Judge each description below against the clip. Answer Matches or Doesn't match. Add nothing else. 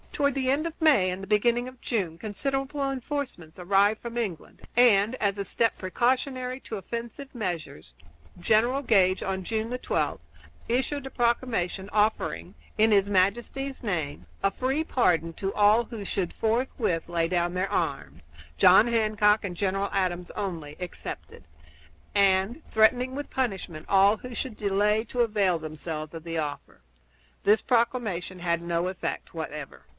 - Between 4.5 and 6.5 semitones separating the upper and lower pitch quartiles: Matches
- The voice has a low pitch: Doesn't match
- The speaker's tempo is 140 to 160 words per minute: Matches